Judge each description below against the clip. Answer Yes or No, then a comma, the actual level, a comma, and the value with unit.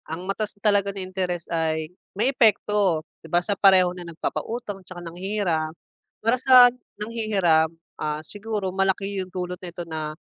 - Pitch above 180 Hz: Yes, high, 190 Hz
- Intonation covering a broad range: No, average, 3.3 semitones